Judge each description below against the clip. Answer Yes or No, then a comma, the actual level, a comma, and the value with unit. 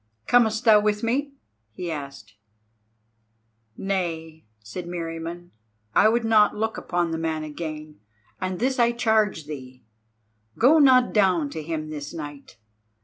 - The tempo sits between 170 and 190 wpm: No, slow, 135 wpm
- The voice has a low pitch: No, medium, 175 Hz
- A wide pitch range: Yes, wide, 6.1 semitones